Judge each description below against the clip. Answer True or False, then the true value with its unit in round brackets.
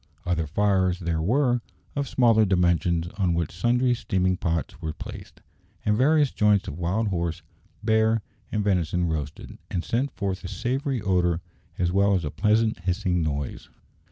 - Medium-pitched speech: False (95 Hz)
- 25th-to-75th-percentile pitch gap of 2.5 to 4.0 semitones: False (4.4 semitones)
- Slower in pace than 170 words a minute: True (155 wpm)